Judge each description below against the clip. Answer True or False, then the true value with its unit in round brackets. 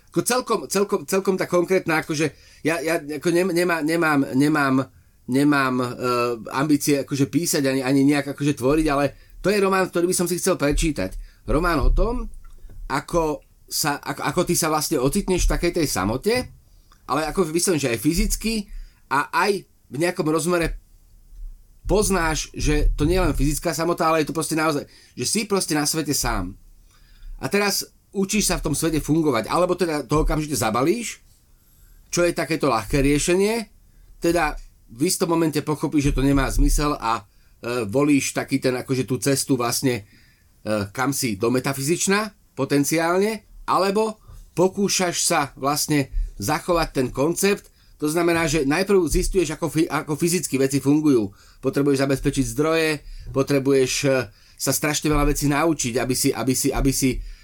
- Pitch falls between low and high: True (150 Hz)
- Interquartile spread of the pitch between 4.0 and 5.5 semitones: True (4.5 semitones)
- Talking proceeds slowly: False (160 wpm)